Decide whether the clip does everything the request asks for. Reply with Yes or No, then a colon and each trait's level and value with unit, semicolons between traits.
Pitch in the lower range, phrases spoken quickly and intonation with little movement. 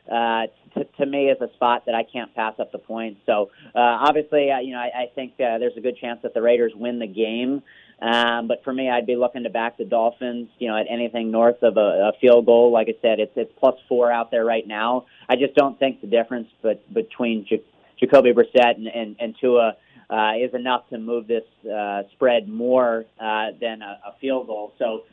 Yes: low, 120 Hz; fast, 230 wpm; narrow, 1.7 semitones